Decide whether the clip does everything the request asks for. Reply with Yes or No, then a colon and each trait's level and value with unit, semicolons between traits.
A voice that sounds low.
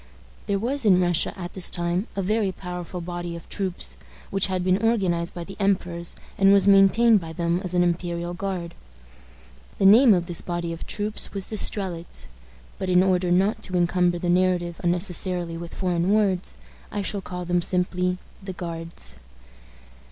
No: medium, 180 Hz